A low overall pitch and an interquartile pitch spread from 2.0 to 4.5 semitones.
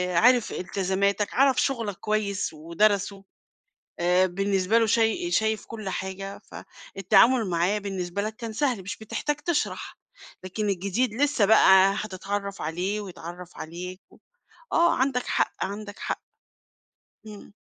No: high, 200 Hz; average, 2.9 semitones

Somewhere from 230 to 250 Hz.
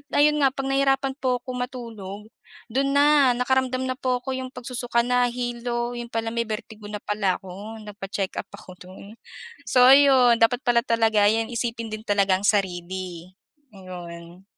Yes: high, 235 Hz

